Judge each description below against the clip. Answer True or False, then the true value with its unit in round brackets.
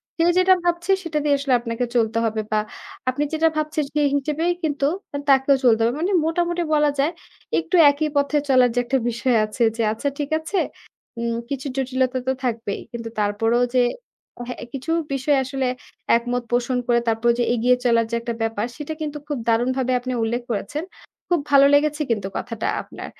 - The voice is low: False (260 Hz)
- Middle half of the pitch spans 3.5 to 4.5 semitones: True (4.1 semitones)